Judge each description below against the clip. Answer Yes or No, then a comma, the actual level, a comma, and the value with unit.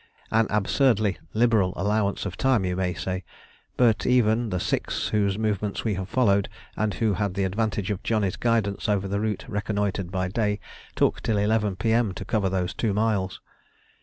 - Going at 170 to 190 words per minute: Yes, average, 175 wpm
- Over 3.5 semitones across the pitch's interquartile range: No, narrow, 2.4 semitones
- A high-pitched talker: No, low, 105 Hz